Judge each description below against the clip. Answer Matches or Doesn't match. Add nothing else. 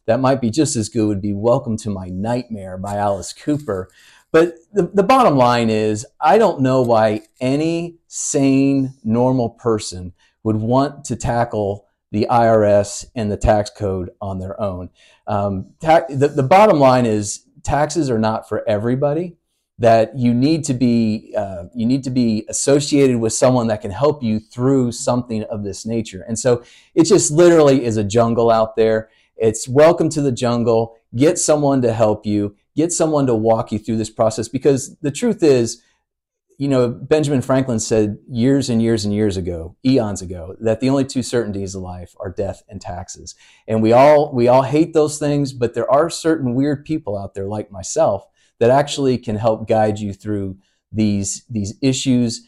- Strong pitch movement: Doesn't match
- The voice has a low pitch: Matches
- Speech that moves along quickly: Doesn't match